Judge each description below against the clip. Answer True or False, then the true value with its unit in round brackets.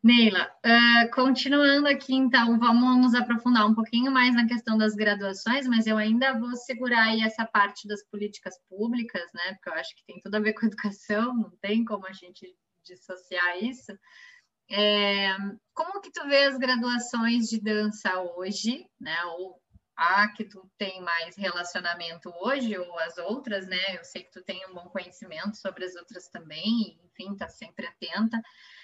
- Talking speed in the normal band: True (175 wpm)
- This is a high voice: True (210 Hz)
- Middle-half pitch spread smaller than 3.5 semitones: False (4.1 semitones)